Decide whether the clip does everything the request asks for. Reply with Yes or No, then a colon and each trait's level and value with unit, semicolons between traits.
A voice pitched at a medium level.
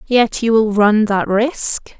No: high, 220 Hz